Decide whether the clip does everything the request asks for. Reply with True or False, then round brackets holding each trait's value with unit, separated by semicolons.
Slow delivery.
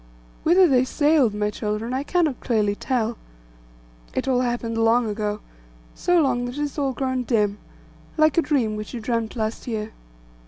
False (170 wpm)